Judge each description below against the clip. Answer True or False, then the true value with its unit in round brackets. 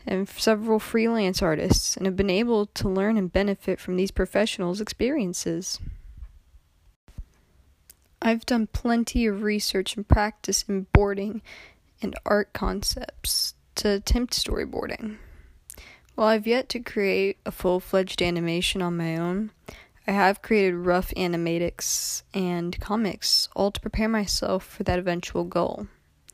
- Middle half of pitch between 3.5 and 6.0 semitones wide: True (3.8 semitones)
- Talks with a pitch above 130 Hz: True (190 Hz)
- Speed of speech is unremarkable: False (130 wpm)